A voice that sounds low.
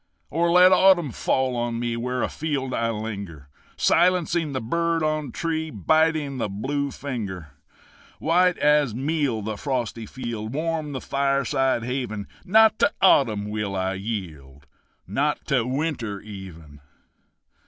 Yes: low, 130 Hz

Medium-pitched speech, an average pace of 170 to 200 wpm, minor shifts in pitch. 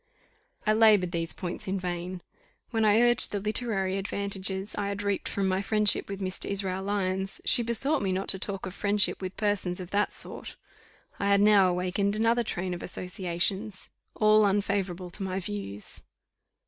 No: high, 195 Hz; average, 175 wpm; narrow, 2.0 semitones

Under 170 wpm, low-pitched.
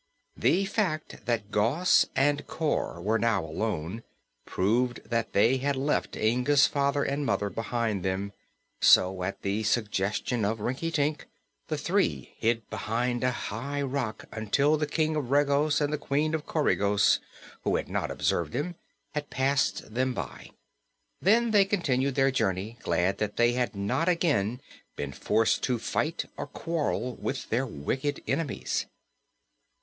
Yes: average, 145 wpm; low, 125 Hz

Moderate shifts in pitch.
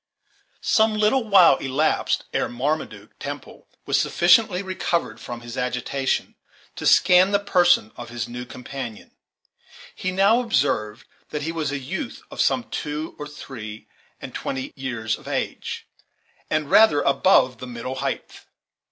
No: wide, 6.9 semitones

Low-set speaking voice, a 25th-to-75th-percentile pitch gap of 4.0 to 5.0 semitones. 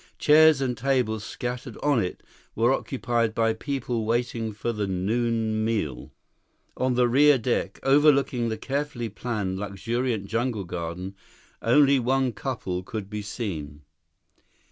No: low, 115 Hz; average, 3.6 semitones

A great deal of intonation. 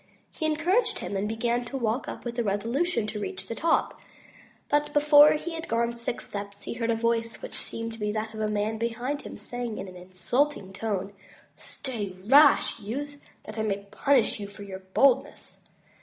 No: average, 5.0 semitones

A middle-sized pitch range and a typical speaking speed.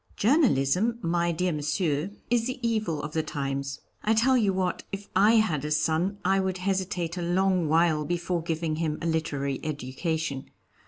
Yes: average, 4.1 semitones; average, 175 wpm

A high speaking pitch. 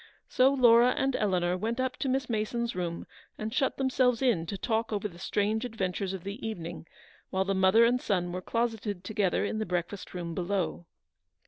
Yes: high, 210 Hz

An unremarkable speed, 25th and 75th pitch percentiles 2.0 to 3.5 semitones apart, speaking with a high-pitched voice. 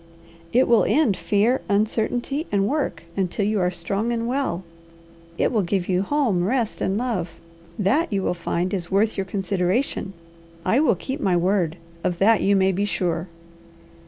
No: average, 170 wpm; average, 4.3 semitones; high, 200 Hz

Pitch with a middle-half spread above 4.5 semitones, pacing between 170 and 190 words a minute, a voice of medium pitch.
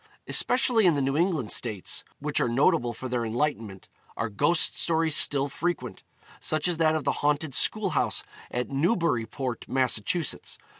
No: average, 5.3 semitones; average, 155 wpm; medium, 145 Hz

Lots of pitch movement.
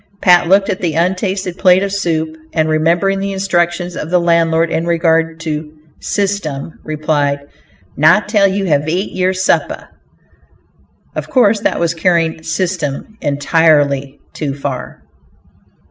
No: average, 3.2 semitones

